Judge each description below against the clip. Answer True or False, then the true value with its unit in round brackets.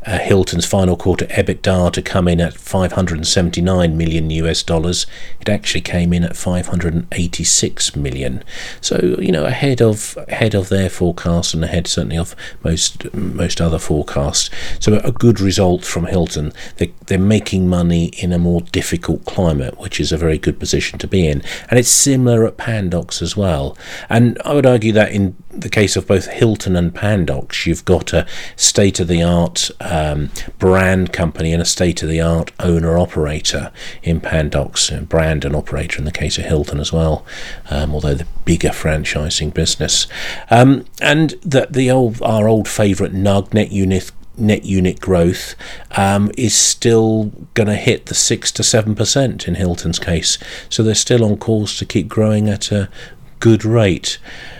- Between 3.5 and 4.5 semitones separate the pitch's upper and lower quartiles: True (4.0 semitones)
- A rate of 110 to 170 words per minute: False (180 wpm)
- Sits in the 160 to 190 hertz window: False (90 Hz)